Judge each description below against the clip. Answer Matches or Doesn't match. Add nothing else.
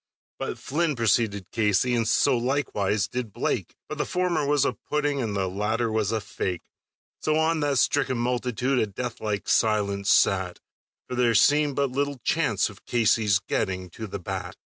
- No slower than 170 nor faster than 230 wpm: Matches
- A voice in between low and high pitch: Doesn't match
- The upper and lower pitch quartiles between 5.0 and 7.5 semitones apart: Matches